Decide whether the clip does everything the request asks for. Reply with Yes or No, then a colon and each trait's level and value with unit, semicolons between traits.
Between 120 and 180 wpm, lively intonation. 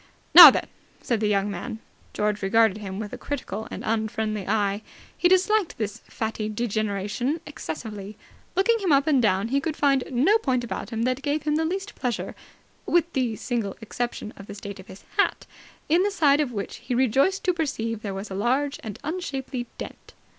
No: average, 195 wpm; wide, 5.7 semitones